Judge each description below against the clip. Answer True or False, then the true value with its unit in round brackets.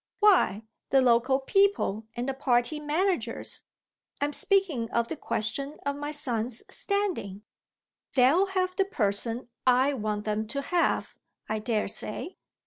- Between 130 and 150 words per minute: True (135 wpm)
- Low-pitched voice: False (265 Hz)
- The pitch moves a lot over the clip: True (6.3 semitones)